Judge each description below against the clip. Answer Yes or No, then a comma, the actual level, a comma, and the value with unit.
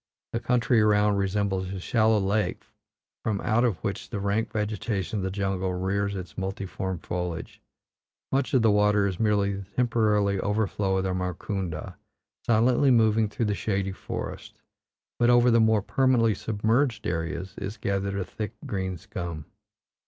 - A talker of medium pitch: No, low, 100 Hz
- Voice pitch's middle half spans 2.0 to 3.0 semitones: Yes, narrow, 2.6 semitones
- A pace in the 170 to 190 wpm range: No, average, 155 wpm